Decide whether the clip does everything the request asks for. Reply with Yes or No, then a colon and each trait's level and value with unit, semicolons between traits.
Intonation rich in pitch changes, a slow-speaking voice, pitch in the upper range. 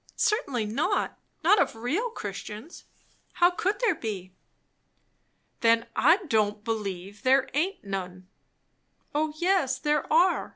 Yes: wide, 8.8 semitones; slow, 120 wpm; very high, 260 Hz